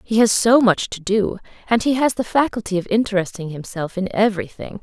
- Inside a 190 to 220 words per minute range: Yes, average, 200 wpm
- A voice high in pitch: Yes, high, 205 Hz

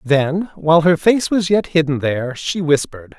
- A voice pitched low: No, medium, 160 Hz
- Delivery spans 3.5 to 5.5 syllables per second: Yes, 4.9 syllables/s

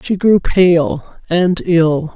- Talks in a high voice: No, medium, 175 Hz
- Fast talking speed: No, average, 140 wpm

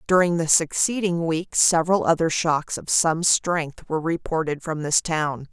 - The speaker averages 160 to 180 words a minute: Yes, average, 165 wpm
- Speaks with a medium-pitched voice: Yes, medium, 165 Hz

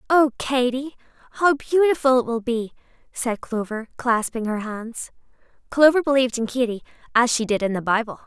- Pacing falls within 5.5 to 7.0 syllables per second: No, 5.2 syllables/s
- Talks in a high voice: Yes, high, 245 Hz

